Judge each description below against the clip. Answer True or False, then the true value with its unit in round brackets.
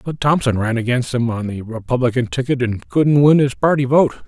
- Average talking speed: False (210 wpm)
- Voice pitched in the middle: False (125 Hz)